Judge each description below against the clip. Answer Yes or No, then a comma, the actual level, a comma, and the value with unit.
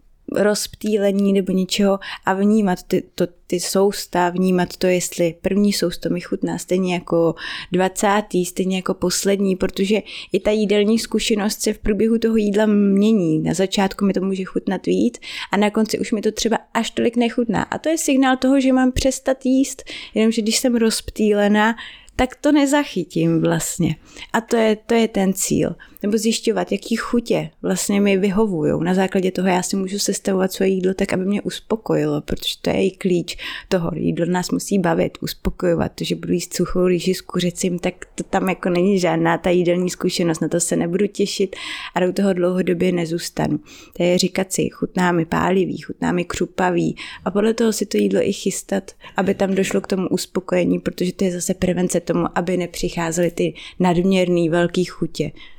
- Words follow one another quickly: Yes, fast, 180 wpm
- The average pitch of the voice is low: No, high, 190 Hz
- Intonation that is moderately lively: Yes, average, 3.0 semitones